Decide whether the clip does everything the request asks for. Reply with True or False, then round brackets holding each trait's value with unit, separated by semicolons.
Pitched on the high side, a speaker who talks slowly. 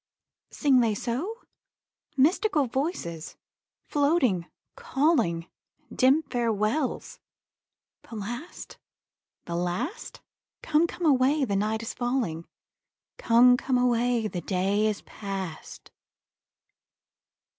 True (240 Hz; 90 wpm)